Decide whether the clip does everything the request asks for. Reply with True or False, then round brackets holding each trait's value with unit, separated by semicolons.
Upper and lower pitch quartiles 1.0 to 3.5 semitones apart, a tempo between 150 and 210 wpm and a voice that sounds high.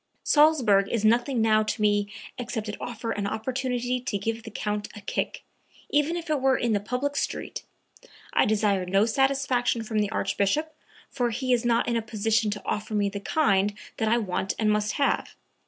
True (3.2 semitones; 190 wpm; 225 Hz)